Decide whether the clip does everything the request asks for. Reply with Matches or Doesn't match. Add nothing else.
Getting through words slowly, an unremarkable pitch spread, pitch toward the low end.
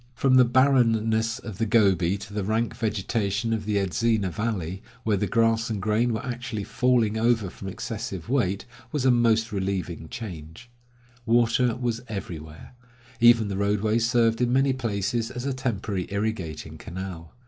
Doesn't match